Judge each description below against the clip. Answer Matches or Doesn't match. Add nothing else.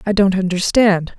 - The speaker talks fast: Doesn't match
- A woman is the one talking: Matches